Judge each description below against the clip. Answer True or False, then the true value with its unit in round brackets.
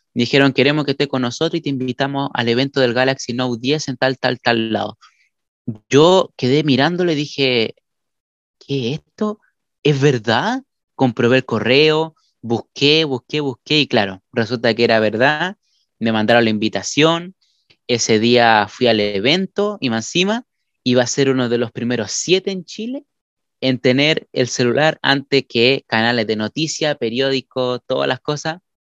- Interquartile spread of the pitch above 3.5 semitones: True (4.0 semitones)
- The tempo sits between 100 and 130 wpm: False (160 wpm)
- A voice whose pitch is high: False (130 Hz)